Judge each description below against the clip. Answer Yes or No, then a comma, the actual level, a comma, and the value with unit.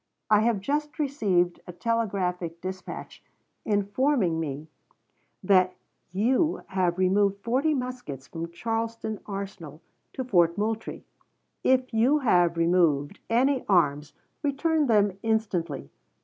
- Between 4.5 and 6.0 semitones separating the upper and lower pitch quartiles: Yes, average, 5.3 semitones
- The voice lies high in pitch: Yes, high, 200 Hz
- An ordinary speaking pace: No, slow, 110 wpm